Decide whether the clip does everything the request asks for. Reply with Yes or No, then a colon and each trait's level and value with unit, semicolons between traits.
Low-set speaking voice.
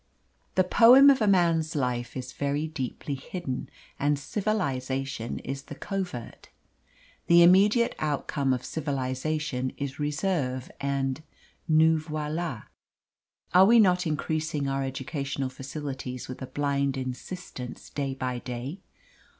No: medium, 145 Hz